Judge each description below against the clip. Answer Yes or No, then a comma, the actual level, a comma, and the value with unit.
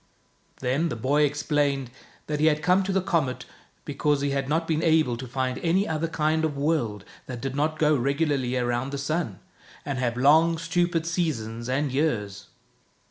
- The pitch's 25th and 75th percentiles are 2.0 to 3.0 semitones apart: No, average, 3.8 semitones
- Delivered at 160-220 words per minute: Yes, average, 180 wpm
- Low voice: No, medium, 145 Hz